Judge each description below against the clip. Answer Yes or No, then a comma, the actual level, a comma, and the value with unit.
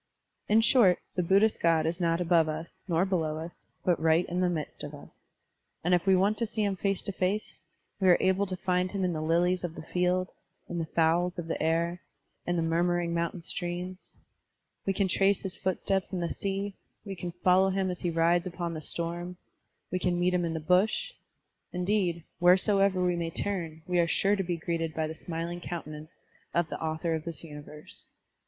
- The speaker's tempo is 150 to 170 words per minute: No, fast, 205 wpm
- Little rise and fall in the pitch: Yes, narrow, 2.1 semitones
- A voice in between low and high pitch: Yes, medium, 175 Hz